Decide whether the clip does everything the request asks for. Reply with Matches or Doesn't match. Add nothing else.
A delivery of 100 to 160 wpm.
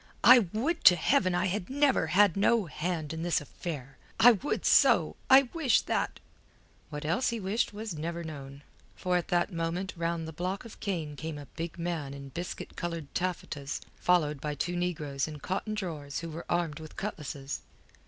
Doesn't match